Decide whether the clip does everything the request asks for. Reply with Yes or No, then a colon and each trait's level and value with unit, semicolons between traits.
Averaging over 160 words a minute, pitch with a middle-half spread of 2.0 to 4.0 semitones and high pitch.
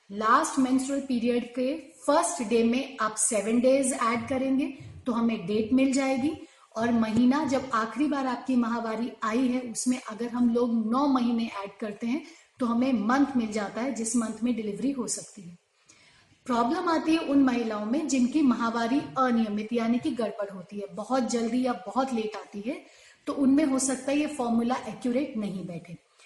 Yes: average, 180 wpm; average, 3.0 semitones; high, 245 Hz